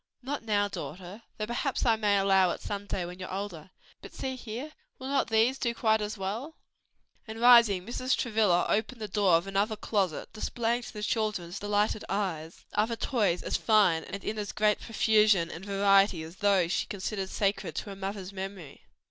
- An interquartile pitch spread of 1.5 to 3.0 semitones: Yes, narrow, 2.6 semitones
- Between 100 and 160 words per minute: No, average, 190 wpm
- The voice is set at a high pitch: Yes, high, 205 Hz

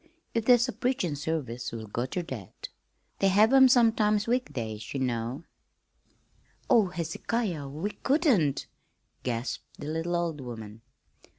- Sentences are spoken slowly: Yes, slow, 130 wpm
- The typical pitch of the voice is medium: Yes, medium, 165 Hz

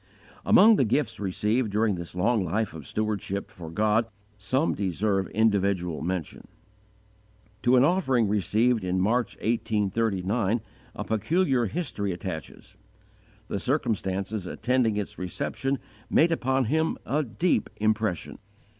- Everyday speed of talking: No, slow, 120 wpm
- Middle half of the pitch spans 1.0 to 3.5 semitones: No, average, 4.4 semitones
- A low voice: Yes, low, 110 Hz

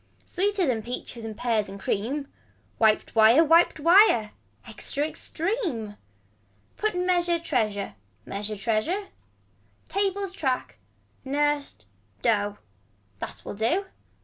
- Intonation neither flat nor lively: No, wide, 8.4 semitones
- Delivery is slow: Yes, slow, 105 wpm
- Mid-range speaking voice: No, very high, 270 Hz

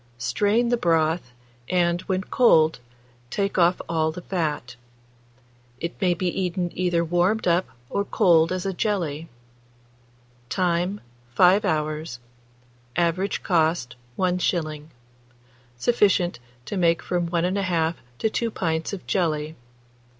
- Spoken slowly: Yes, slow, 120 wpm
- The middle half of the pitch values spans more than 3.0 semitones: No, average, 2.7 semitones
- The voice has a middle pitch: Yes, medium, 175 Hz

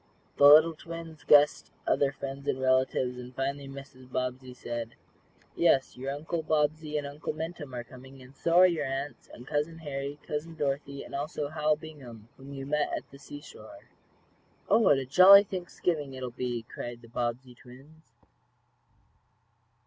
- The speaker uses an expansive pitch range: No, average, 3.0 semitones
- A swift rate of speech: No, average, 165 wpm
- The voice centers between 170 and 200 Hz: No, medium, 140 Hz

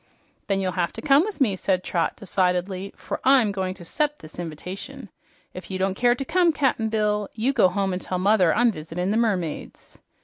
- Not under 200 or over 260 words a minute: Yes, fast, 205 wpm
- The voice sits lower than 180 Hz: No, high, 195 Hz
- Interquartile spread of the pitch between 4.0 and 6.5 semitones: Yes, average, 4.5 semitones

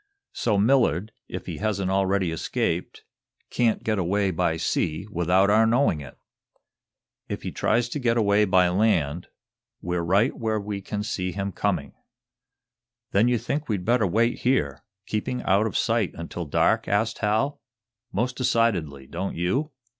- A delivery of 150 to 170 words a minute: Yes, average, 155 wpm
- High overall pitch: No, low, 100 Hz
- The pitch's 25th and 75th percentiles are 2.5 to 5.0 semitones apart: Yes, average, 4.1 semitones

